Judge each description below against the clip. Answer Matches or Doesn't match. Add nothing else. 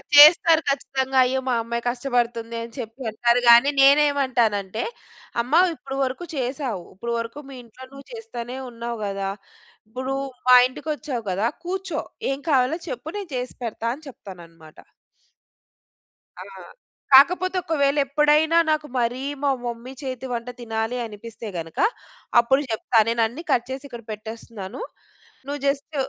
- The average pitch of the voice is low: Doesn't match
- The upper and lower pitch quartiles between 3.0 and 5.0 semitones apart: Matches